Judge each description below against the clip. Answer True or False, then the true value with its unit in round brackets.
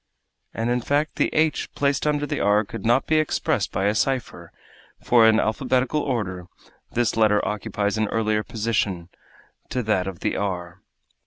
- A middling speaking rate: True (165 wpm)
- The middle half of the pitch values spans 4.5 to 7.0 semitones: False (4.0 semitones)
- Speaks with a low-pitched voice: True (110 Hz)